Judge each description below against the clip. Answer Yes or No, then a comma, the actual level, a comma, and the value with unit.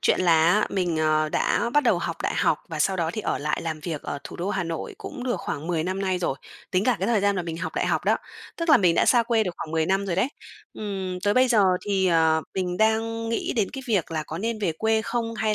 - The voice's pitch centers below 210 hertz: Yes, high, 190 Hz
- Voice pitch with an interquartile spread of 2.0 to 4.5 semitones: No, average, 4.9 semitones